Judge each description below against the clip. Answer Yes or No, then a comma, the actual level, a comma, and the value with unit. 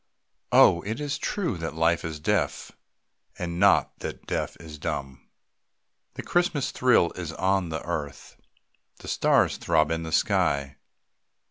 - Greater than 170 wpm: No, average, 140 wpm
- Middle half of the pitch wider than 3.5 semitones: Yes, average, 4.1 semitones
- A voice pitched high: No, very low, 85 Hz